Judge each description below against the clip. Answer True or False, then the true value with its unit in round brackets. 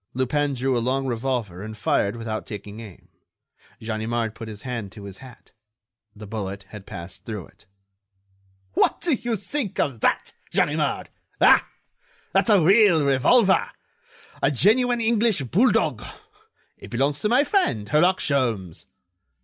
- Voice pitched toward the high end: False (125 Hz)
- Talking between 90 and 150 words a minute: True (140 wpm)